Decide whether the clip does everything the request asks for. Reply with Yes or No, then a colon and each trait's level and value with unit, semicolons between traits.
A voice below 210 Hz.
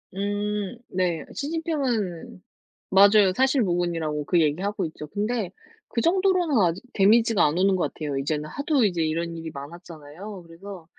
Yes: high, 190 Hz